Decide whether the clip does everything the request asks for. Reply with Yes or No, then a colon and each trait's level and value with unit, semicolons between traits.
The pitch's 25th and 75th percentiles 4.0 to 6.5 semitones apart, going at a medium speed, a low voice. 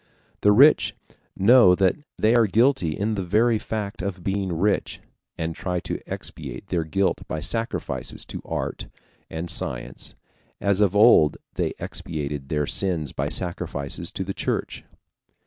Yes: average, 4.3 semitones; average, 145 wpm; very low, 95 Hz